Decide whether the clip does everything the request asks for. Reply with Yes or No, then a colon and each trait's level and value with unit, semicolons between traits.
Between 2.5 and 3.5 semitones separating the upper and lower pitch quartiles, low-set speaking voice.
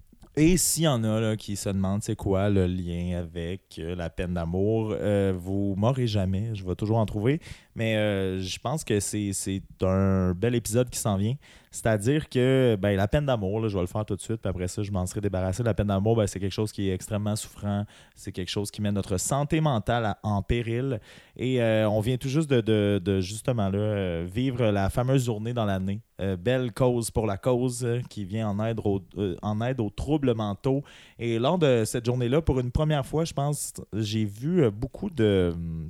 No: average, 4.0 semitones; low, 105 Hz